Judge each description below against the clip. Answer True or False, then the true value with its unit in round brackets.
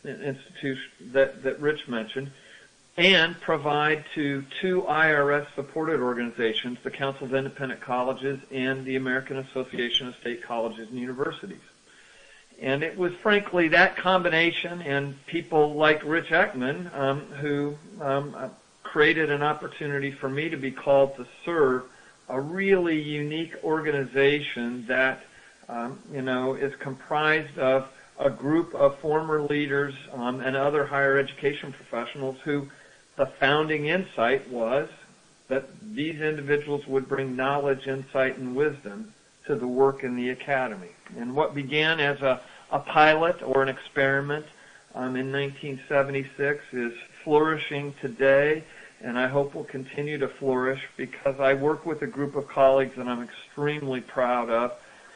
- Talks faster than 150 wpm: False (135 wpm)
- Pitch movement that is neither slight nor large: False (2.3 semitones)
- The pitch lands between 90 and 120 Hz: False (140 Hz)